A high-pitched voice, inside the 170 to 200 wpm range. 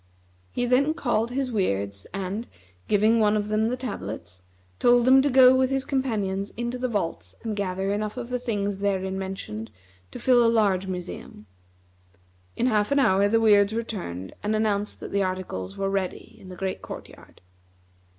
Yes: high, 210 Hz; average, 180 wpm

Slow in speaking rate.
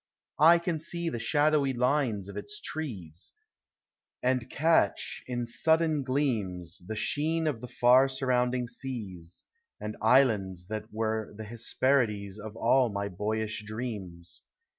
Yes: slow, 130 wpm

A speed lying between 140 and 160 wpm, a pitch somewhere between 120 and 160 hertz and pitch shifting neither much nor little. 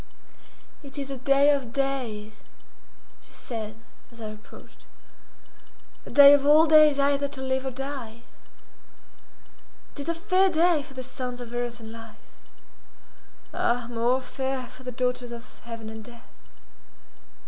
No: average, 145 wpm; very high, 260 Hz; average, 3.2 semitones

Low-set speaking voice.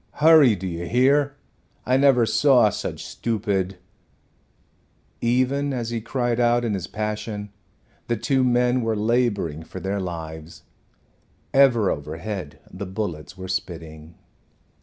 Yes: low, 110 Hz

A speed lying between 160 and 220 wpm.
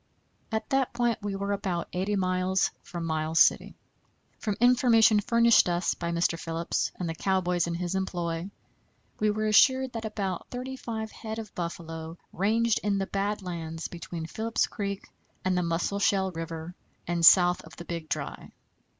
Yes: average, 165 wpm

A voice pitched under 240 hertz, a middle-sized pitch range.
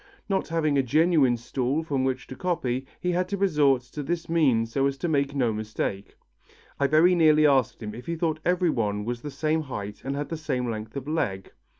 Yes: medium, 140 Hz; average, 4.8 semitones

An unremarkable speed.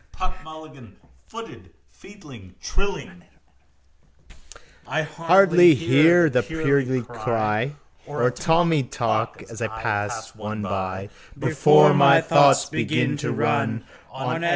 No: slow, 115 wpm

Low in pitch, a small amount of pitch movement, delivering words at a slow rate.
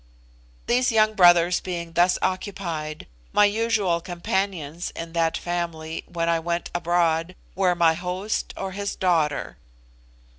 No: medium, 175 Hz; narrow, 2.3 semitones; slow, 125 wpm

